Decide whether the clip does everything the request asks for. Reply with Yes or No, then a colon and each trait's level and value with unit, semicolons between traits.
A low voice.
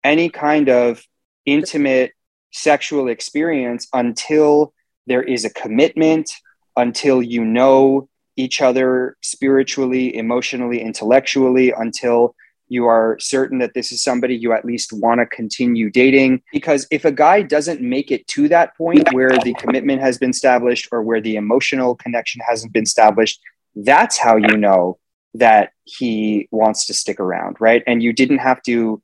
Yes: low, 125 Hz